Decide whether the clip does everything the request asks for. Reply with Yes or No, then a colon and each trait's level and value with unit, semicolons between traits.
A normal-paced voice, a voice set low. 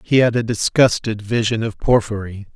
Yes: average, 165 wpm; low, 110 Hz